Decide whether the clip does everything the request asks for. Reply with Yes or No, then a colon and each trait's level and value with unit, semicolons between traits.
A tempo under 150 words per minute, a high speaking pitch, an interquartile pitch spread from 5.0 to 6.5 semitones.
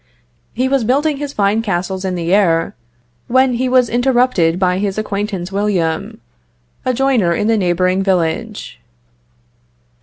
Yes: average, 140 wpm; high, 205 Hz; average, 5.3 semitones